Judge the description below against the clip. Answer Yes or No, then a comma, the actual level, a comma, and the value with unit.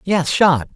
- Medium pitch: Yes, medium, 165 Hz